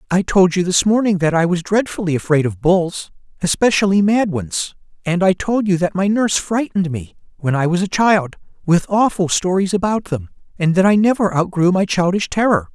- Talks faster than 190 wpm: Yes, average, 200 wpm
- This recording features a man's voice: Yes, male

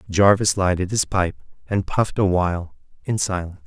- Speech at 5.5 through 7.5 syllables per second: Yes, 5.7 syllables/s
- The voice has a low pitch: Yes, very low, 95 Hz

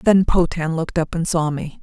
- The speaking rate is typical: No, fast, 230 wpm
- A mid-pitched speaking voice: Yes, medium, 165 Hz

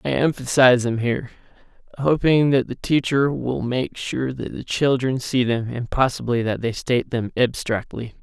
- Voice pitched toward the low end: Yes, low, 125 Hz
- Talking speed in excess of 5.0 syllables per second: No, 4.8 syllables/s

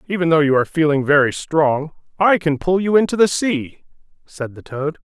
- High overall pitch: No, medium, 160 Hz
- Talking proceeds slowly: No, average, 200 wpm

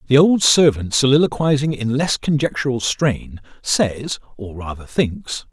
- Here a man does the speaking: Yes, male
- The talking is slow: Yes, slow, 130 wpm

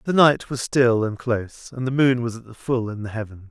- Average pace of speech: No, fast, 275 wpm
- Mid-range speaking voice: No, low, 120 Hz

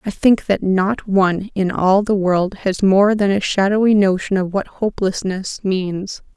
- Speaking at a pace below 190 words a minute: Yes, average, 180 wpm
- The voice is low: No, high, 195 Hz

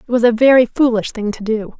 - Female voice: Yes, female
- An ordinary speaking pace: No, fast, 265 wpm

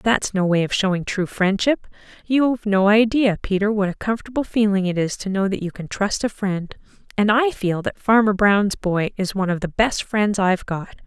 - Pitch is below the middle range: No, high, 200 Hz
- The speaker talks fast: Yes, fast, 215 wpm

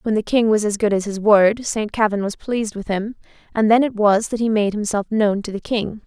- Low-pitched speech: No, high, 210 Hz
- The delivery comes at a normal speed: No, fast, 265 wpm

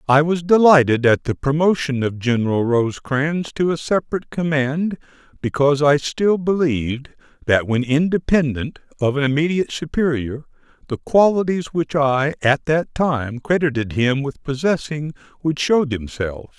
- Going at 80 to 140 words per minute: Yes, slow, 135 wpm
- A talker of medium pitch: Yes, medium, 145 Hz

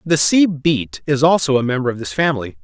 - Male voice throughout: Yes, male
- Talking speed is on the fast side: Yes, fast, 230 wpm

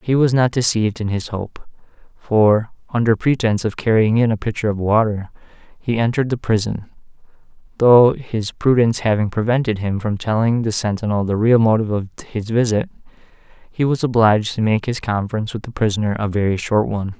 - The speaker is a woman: No, male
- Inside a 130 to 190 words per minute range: Yes, average, 180 wpm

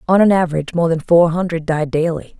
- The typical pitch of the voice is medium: Yes, medium, 165 Hz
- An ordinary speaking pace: No, fast, 225 wpm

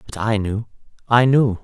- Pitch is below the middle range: Yes, low, 110 Hz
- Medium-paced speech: Yes, average, 185 wpm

